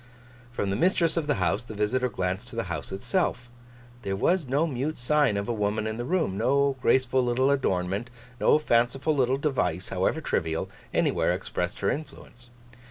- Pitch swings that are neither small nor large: No, wide, 5.7 semitones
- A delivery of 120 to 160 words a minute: No, average, 175 wpm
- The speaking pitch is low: Yes, low, 125 Hz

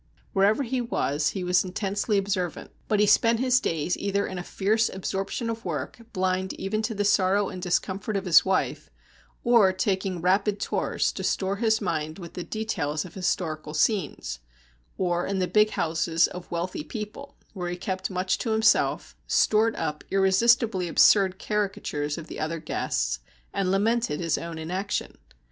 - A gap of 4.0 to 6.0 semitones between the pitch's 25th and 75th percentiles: No, average, 3.2 semitones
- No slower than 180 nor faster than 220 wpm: No, average, 165 wpm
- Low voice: No, high, 190 Hz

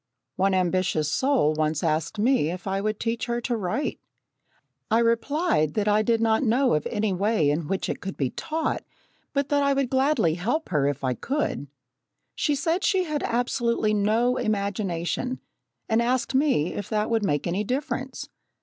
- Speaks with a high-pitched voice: Yes, high, 220 Hz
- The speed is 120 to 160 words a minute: No, average, 175 wpm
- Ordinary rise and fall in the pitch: No, wide, 6.3 semitones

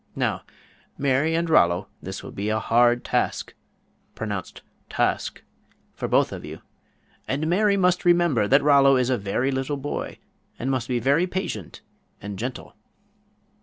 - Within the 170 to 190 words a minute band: No, average, 150 wpm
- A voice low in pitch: Yes, low, 130 Hz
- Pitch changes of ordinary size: No, wide, 6.0 semitones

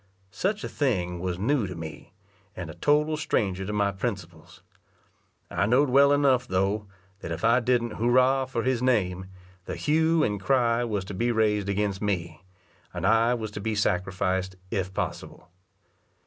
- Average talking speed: Yes, average, 165 wpm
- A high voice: No, low, 105 Hz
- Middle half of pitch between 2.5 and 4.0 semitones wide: No, average, 5.1 semitones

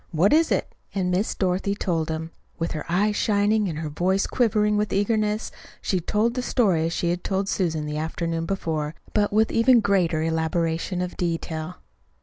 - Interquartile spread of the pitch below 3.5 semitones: No, average, 4.2 semitones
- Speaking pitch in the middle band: Yes, medium, 180 Hz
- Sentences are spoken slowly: No, average, 190 wpm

